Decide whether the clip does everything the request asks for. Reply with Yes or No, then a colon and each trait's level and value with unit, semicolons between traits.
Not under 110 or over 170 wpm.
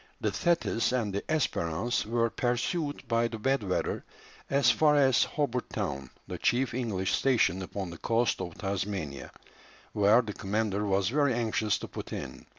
Yes: average, 160 wpm